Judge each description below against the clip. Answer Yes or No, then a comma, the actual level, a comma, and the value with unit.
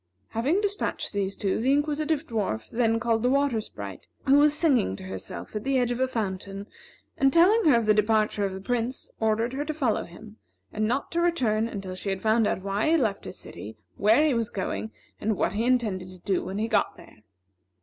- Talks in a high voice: Yes, high, 225 Hz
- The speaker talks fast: Yes, fast, 220 wpm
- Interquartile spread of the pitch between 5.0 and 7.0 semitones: Yes, average, 5.3 semitones